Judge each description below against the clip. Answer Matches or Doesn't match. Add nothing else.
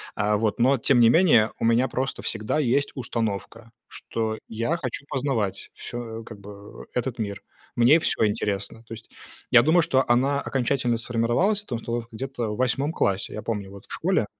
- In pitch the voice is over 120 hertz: Doesn't match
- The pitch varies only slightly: Doesn't match